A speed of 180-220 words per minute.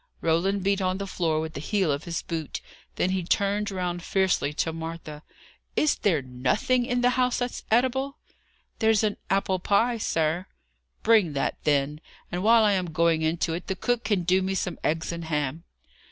Yes: average, 185 wpm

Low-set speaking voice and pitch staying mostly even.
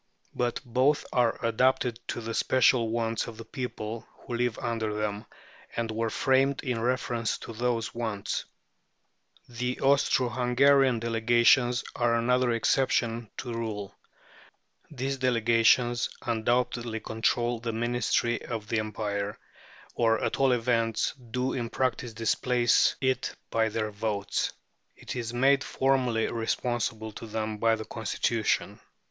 Yes: low, 115 Hz; narrow, 1.8 semitones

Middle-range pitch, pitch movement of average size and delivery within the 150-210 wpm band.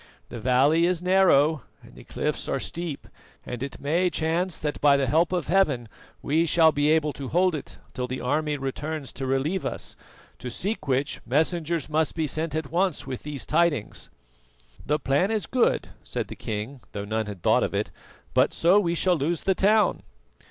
Yes: medium, 155 Hz; average, 4.0 semitones; average, 190 wpm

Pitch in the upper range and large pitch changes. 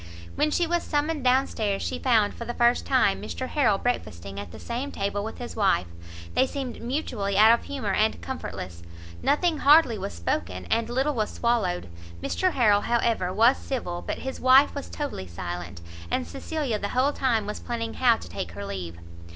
Yes: high, 230 Hz; wide, 5.8 semitones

